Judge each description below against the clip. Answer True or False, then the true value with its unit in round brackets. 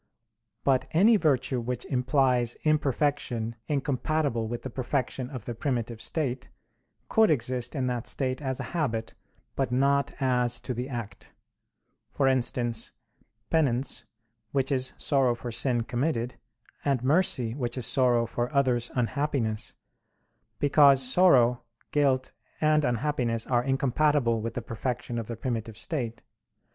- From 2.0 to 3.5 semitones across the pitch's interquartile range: True (2.8 semitones)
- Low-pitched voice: True (130 Hz)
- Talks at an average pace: False (130 wpm)